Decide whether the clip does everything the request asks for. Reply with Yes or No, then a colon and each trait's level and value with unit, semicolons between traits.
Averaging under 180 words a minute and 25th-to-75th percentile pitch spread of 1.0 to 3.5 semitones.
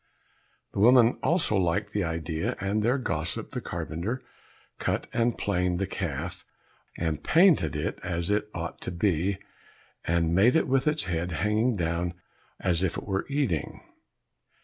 No: average, 150 wpm; average, 4.6 semitones